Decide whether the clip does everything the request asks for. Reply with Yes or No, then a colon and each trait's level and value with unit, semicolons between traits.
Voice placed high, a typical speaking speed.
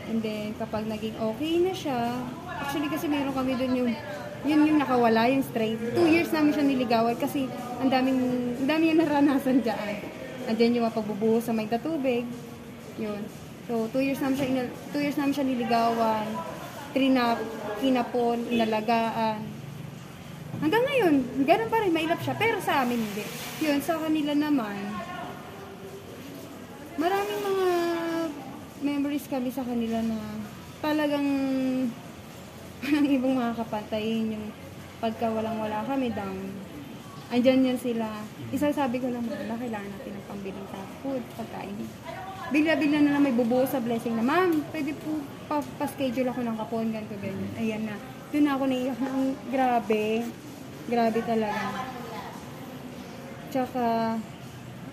Yes: very high, 255 Hz; average, 140 wpm